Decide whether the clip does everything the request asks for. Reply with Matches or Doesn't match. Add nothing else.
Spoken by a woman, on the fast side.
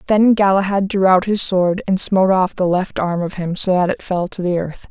Matches